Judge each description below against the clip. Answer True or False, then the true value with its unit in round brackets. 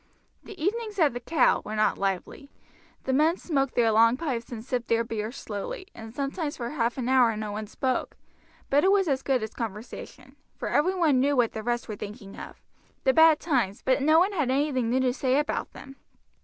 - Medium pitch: False (260 Hz)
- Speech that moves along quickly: True (210 wpm)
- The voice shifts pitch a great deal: False (4.6 semitones)